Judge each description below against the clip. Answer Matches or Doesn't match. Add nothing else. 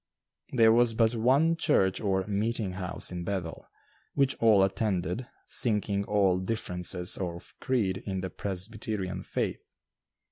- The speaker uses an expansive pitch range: Doesn't match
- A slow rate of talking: Matches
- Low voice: Matches